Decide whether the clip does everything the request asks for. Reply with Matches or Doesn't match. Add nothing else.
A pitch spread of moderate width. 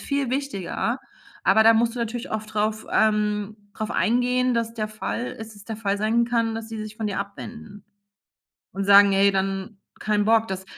Doesn't match